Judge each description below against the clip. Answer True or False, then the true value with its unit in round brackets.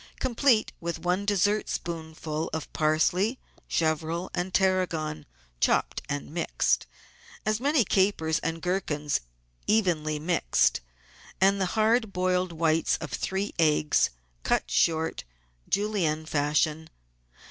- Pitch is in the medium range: True (170 Hz)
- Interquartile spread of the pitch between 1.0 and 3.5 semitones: False (3.9 semitones)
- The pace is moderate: False (105 wpm)